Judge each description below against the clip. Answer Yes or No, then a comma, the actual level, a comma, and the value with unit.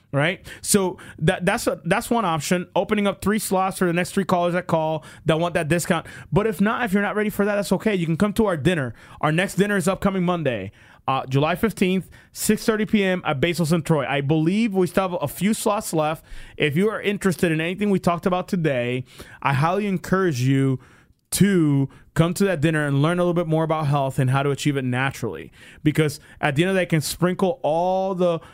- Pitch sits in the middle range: Yes, medium, 175 Hz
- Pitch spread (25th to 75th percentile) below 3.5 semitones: No, average, 4.4 semitones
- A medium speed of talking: No, fast, 230 wpm